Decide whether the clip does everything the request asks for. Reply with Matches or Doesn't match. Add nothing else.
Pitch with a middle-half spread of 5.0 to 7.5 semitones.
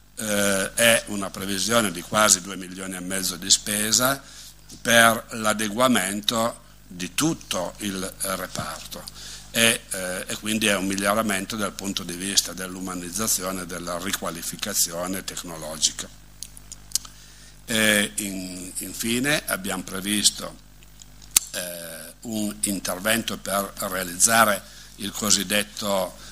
Doesn't match